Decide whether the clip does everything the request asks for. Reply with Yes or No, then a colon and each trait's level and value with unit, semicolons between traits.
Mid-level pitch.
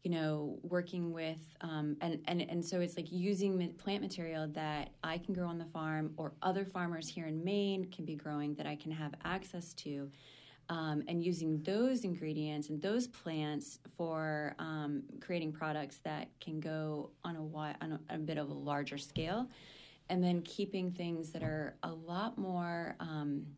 Yes: medium, 160 Hz